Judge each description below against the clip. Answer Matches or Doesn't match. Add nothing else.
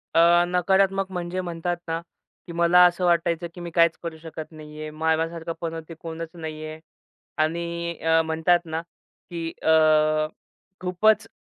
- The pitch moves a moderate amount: Doesn't match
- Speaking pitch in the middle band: Matches